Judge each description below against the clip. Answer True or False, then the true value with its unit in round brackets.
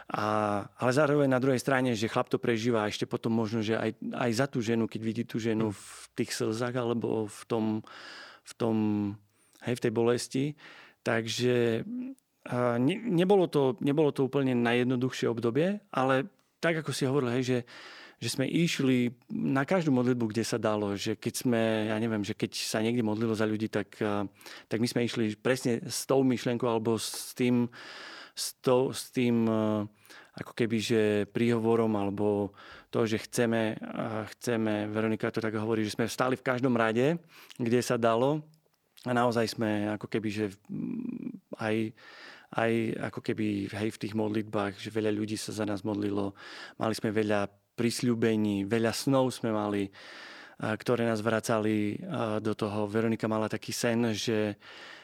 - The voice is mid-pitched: False (115 Hz)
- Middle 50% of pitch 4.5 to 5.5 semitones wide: False (2.7 semitones)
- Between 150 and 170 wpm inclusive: True (165 wpm)